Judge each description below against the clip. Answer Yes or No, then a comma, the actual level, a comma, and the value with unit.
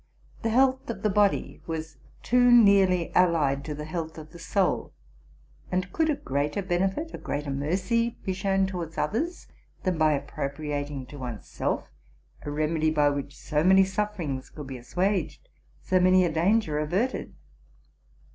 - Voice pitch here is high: No, medium, 175 Hz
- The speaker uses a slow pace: No, average, 155 wpm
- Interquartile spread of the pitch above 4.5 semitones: Yes, average, 4.9 semitones